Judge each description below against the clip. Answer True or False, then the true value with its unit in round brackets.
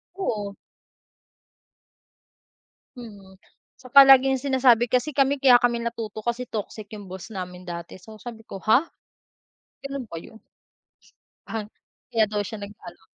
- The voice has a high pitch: True (225 Hz)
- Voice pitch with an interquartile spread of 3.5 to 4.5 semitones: True (3.8 semitones)